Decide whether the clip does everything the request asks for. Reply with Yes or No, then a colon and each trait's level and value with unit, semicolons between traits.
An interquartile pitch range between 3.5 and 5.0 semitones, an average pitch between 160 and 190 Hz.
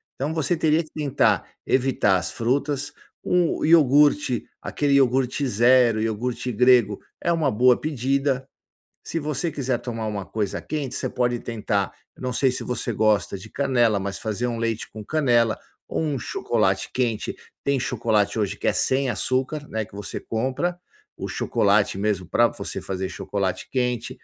No: average, 4.1 semitones; low, 125 Hz